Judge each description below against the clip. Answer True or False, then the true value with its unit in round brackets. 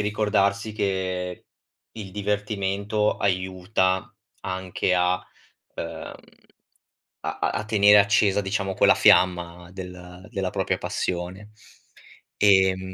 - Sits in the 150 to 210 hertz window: False (95 Hz)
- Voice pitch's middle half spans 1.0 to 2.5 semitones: True (2.0 semitones)